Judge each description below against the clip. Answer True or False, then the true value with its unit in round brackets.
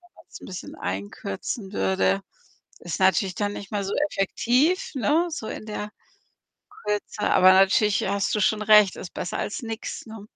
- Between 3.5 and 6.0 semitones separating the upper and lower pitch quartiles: False (2.7 semitones)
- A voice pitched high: True (205 Hz)